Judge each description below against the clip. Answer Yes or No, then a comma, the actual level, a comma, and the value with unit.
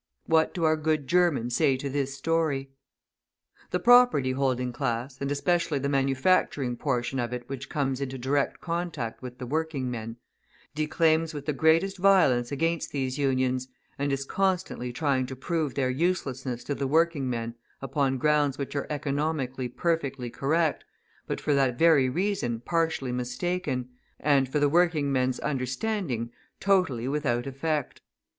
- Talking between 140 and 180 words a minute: Yes, average, 155 wpm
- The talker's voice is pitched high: No, medium, 140 Hz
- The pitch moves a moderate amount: Yes, average, 3.8 semitones